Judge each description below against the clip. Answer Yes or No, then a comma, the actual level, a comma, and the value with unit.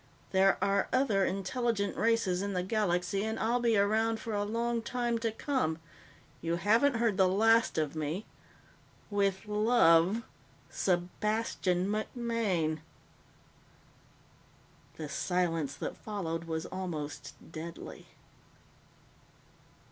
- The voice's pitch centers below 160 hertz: No, high, 200 Hz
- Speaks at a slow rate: Yes, slow, 110 wpm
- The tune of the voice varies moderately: Yes, average, 4.2 semitones